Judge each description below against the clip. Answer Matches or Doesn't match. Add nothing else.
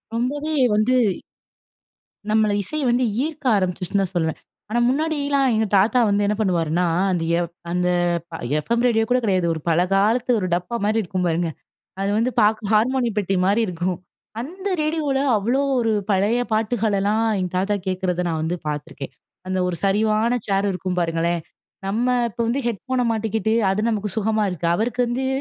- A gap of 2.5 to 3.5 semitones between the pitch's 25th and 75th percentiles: Doesn't match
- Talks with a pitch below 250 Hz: Matches